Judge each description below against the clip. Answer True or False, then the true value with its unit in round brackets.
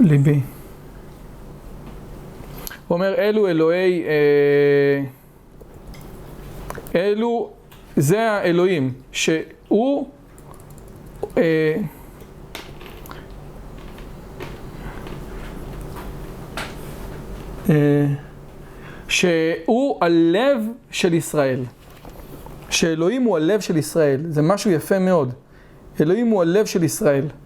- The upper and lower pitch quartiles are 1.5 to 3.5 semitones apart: False (5.1 semitones)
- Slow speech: True (60 wpm)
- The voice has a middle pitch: True (165 Hz)